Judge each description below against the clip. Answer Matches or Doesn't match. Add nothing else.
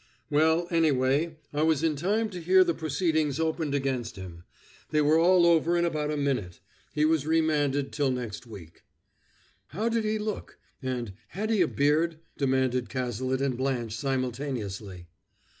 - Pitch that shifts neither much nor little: Matches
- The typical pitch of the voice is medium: Matches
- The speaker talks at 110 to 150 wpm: Doesn't match